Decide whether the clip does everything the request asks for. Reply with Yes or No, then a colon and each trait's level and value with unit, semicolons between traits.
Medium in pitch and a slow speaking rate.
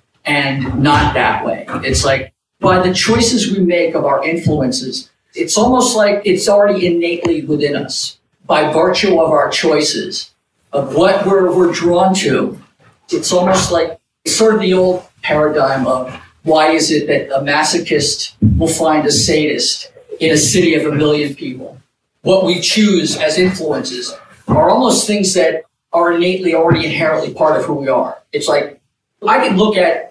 No: medium, 170 Hz; average, 165 wpm